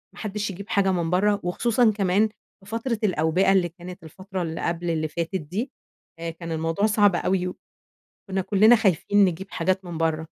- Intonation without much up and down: No, average, 3.4 semitones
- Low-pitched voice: No, medium, 185 Hz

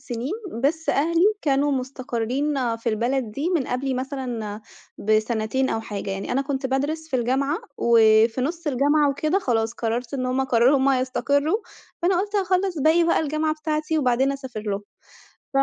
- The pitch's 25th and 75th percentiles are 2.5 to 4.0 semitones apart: No, average, 4.4 semitones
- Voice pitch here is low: No, very high, 265 Hz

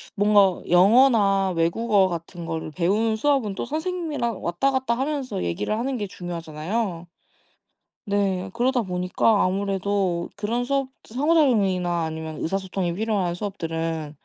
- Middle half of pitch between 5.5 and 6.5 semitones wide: No, average, 5.1 semitones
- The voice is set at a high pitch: Yes, high, 195 Hz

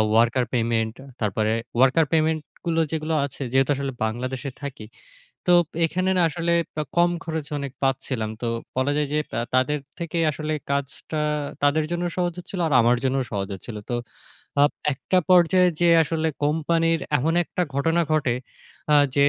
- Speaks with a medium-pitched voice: Yes, medium, 150 Hz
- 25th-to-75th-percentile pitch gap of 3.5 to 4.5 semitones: Yes, average, 4.2 semitones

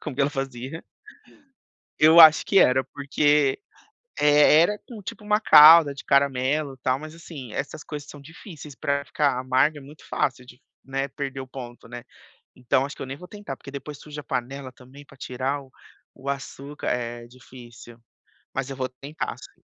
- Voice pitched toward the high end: No, medium, 140 Hz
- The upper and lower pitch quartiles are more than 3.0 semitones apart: No, narrow, 2.5 semitones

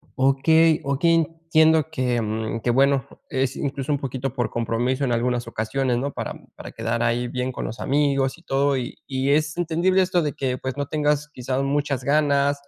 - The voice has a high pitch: No, low, 135 Hz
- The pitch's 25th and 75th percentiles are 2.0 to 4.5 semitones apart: Yes, average, 2.9 semitones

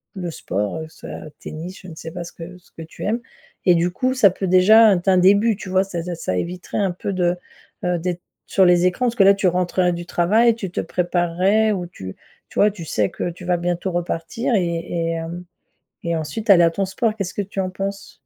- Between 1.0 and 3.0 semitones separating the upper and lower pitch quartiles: Yes, narrow, 2.4 semitones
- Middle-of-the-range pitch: Yes, medium, 180 Hz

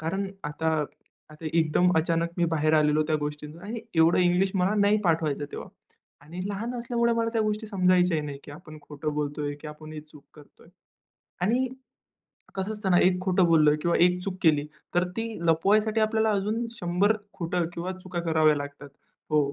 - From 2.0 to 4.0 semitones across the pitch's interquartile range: No, average, 4.5 semitones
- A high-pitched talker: No, medium, 175 Hz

